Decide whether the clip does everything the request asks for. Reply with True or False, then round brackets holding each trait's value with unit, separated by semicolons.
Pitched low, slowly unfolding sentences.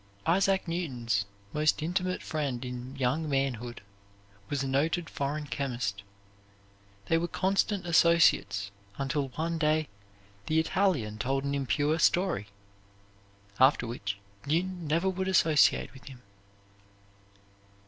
False (150 Hz; 115 wpm)